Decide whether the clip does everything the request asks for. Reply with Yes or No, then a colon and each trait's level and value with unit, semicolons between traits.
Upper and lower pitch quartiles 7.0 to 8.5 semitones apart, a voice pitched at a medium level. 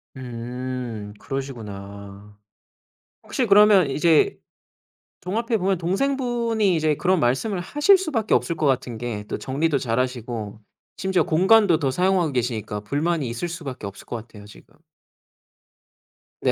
Yes: wide, 8.2 semitones; medium, 145 Hz